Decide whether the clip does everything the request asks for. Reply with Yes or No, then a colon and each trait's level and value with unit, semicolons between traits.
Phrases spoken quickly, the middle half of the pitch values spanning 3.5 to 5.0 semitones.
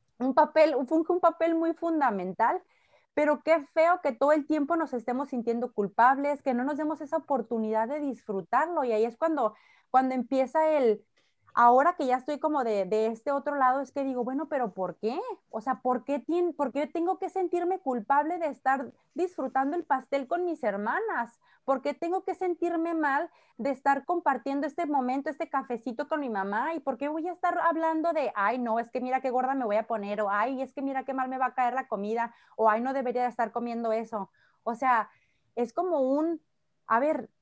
Yes: fast, 210 wpm; average, 4.6 semitones